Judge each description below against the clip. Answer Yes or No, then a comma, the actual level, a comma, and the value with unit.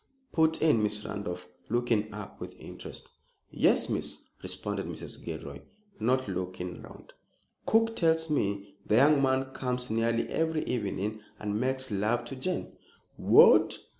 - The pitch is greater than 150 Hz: No, low, 115 Hz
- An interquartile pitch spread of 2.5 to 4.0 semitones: No, average, 4.5 semitones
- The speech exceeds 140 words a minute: No, slow, 135 wpm